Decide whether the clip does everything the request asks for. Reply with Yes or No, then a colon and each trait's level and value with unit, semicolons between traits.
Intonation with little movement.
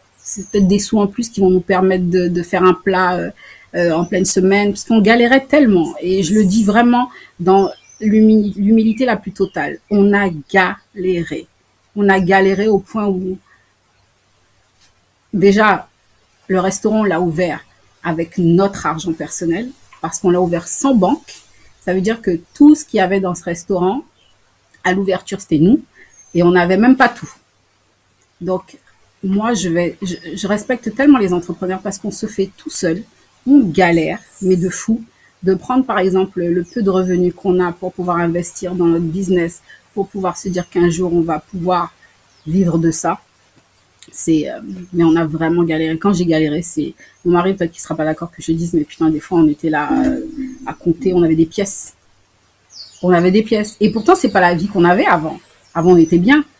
No: average, 3.3 semitones